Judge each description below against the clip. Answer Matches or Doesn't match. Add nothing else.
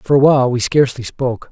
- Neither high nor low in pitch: Doesn't match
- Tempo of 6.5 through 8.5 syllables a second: Matches